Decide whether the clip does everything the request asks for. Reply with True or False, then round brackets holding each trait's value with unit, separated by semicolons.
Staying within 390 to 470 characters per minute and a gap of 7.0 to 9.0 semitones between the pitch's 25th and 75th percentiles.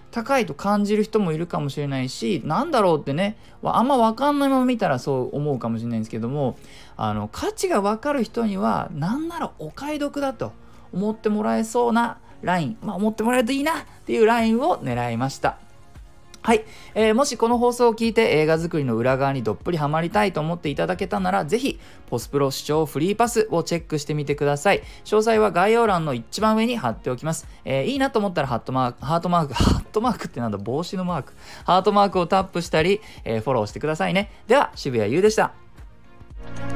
True (450 characters per minute; 8.2 semitones)